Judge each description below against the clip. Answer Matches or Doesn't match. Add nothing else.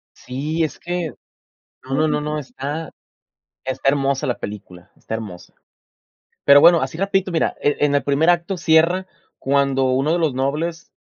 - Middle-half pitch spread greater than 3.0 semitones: Matches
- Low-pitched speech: Doesn't match